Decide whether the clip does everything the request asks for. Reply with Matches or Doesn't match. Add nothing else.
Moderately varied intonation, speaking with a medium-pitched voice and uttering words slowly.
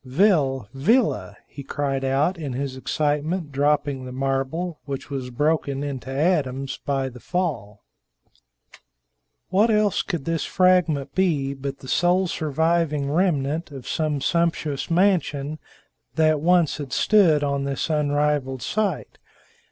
Matches